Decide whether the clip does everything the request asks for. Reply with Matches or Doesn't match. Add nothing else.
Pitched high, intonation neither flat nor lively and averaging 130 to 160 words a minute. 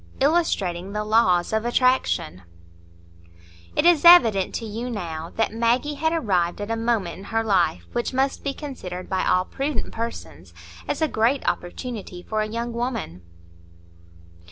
Doesn't match